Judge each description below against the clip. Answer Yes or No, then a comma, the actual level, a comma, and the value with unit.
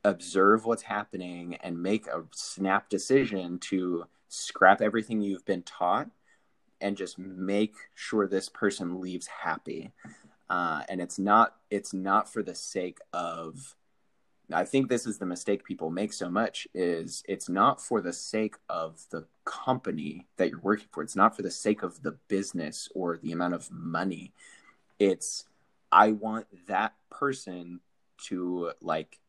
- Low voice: Yes, very low, 95 Hz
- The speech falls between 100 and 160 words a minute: Yes, average, 150 wpm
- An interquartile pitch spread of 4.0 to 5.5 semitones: No, average, 3.2 semitones